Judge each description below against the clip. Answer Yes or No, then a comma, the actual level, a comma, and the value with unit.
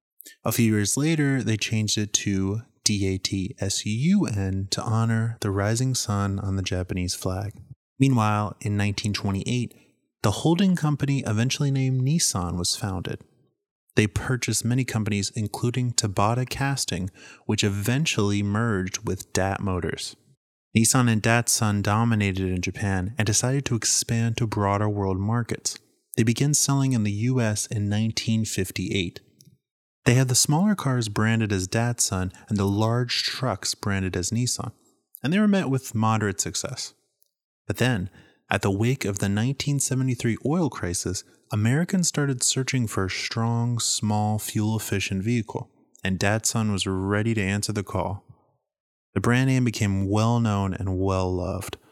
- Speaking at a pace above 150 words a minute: No, average, 140 wpm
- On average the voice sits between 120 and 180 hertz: No, low, 110 Hz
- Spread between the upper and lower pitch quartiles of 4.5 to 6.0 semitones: No, average, 3.8 semitones